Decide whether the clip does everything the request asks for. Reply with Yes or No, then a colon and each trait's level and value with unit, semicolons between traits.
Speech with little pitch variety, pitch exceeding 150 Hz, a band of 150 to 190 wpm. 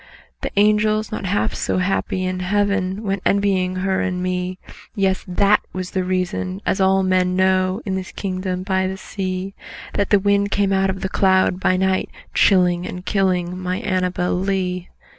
Yes: narrow, 1.3 semitones; high, 190 Hz; average, 165 wpm